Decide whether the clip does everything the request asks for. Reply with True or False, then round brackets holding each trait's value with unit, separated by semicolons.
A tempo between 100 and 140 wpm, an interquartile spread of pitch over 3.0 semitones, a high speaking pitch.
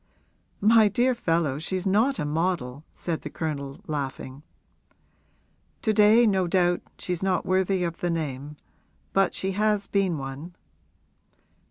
False (135 wpm; 4.8 semitones; 175 Hz)